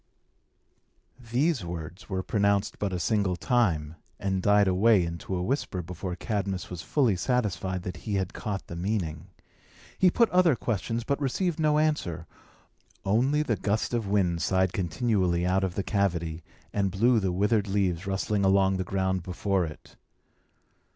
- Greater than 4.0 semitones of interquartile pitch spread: No, average, 3.7 semitones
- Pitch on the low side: Yes, very low, 95 Hz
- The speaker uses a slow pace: No, average, 155 wpm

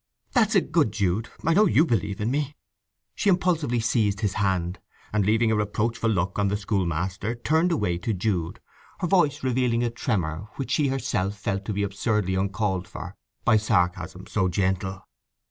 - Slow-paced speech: No, average, 170 wpm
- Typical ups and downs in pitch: Yes, average, 5.0 semitones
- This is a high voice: No, low, 105 Hz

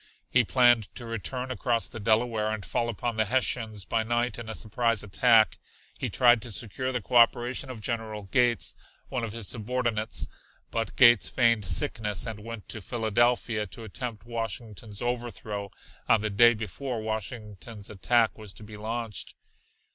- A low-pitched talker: Yes, low, 115 Hz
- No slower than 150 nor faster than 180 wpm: Yes, average, 160 wpm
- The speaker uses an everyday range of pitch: No, narrow, 2.0 semitones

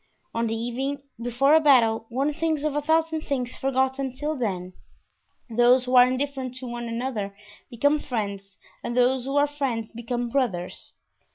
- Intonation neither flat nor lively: Yes, average, 3.2 semitones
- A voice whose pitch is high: Yes, very high, 255 Hz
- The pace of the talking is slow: No, average, 165 wpm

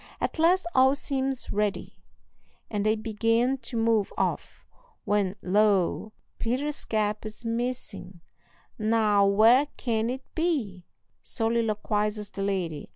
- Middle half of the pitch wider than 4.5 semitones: No, average, 3.1 semitones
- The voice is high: Yes, high, 220 Hz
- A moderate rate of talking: No, slow, 115 wpm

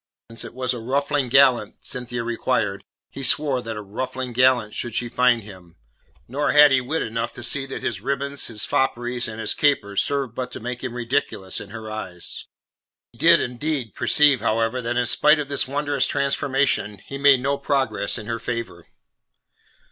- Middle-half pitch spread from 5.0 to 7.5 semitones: No, average, 3.4 semitones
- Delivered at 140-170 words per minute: No, average, 185 wpm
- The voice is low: Yes, low, 125 Hz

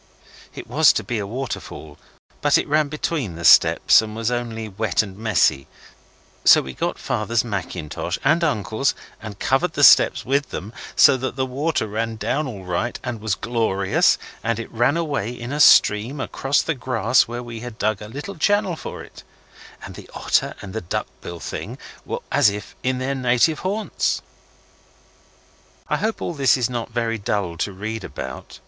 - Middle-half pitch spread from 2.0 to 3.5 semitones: No, average, 4.4 semitones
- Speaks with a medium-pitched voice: No, low, 115 Hz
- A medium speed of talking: Yes, average, 180 wpm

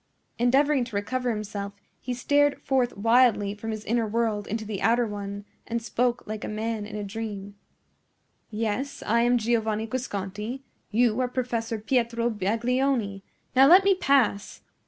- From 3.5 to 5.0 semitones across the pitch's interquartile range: No, average, 2.9 semitones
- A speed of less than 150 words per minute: No, average, 155 wpm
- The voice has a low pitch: No, high, 230 Hz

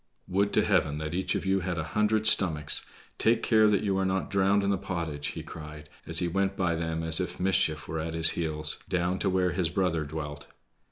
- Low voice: Yes, very low, 90 Hz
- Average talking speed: No, fast, 225 wpm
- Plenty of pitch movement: No, average, 3.4 semitones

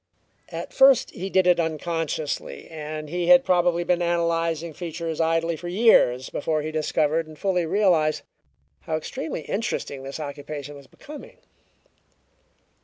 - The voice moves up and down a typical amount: No, narrow, 2.3 semitones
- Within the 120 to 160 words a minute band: Yes, slow, 135 wpm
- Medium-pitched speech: Yes, medium, 165 Hz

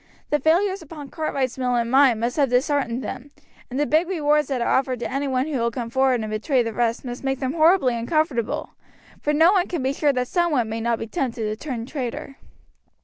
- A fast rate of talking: Yes, fast, 230 wpm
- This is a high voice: Yes, very high, 265 Hz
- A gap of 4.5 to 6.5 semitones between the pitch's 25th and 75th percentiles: No, average, 3.8 semitones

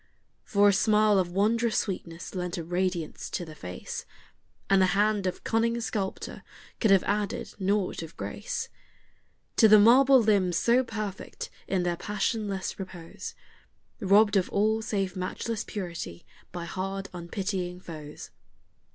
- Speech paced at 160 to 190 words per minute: No, average, 140 wpm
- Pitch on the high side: Yes, high, 195 Hz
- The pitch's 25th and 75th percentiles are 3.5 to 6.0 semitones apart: No, average, 3.1 semitones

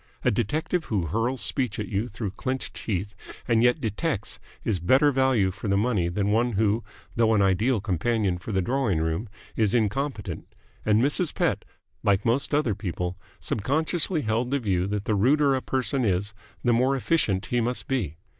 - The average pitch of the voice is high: No, low, 110 Hz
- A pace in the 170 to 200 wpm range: Yes, average, 180 wpm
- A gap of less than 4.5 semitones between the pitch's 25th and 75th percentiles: No, average, 4.8 semitones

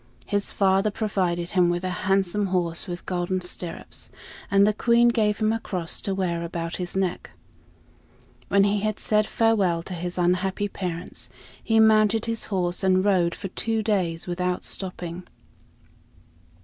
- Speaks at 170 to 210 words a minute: No, average, 155 wpm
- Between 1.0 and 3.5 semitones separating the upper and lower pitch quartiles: Yes, average, 3.0 semitones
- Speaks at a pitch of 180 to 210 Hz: Yes, high, 190 Hz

